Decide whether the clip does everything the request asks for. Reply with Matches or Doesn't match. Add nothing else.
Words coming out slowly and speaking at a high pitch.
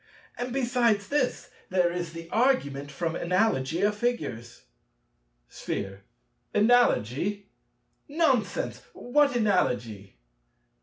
Matches